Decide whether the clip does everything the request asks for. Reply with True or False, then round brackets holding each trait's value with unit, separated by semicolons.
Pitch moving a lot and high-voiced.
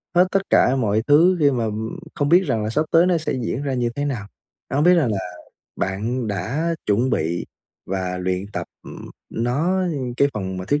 False (7.0 semitones; 125 Hz)